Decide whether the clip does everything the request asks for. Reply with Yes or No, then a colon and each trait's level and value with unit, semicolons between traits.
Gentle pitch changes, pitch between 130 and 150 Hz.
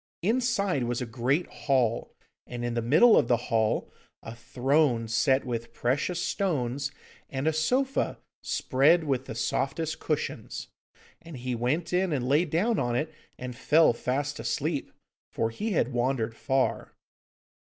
No: average, 4.9 semitones; low, 135 Hz